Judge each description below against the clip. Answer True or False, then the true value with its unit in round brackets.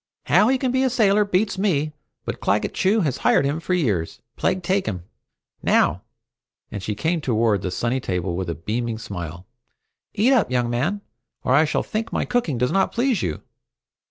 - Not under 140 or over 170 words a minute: False (190 wpm)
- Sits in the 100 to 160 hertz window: True (140 Hz)